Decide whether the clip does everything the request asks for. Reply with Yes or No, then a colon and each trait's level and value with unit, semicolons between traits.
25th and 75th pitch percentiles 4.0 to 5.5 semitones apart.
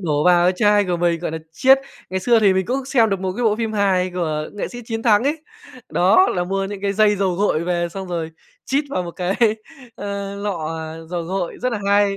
No: average, 3.3 semitones